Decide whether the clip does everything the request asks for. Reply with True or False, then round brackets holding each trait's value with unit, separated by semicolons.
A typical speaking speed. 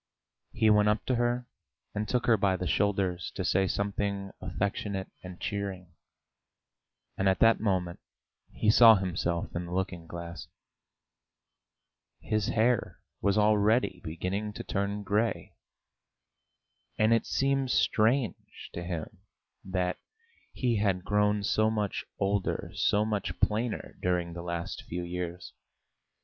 False (130 wpm)